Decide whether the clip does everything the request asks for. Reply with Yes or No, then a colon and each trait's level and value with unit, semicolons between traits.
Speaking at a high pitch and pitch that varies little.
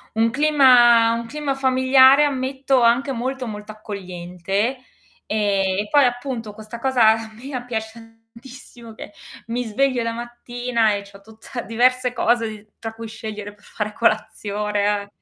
No: high, 230 Hz; average, 3.2 semitones